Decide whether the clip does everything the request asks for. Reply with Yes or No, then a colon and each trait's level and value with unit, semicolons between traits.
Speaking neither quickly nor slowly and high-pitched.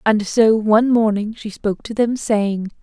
Yes: average, 190 wpm; high, 215 Hz